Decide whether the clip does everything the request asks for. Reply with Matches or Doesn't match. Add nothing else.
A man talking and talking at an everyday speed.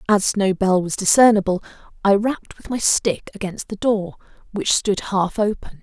Doesn't match